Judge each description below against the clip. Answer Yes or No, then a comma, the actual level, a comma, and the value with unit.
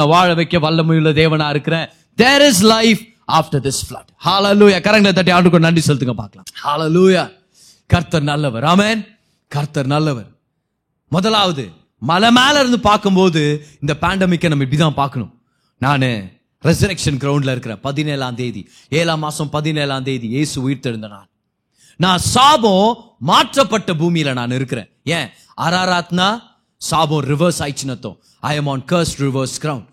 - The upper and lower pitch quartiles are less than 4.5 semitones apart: No, average, 4.9 semitones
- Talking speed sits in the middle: No, fast, 135 wpm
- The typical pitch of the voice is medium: Yes, medium, 155 Hz